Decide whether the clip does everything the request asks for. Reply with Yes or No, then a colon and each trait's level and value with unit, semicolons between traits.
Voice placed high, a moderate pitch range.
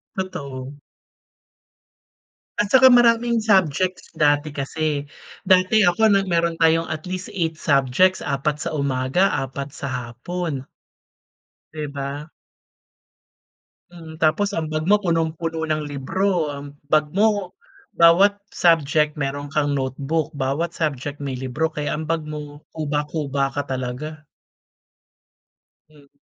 No: medium, 155 Hz; average, 3.6 semitones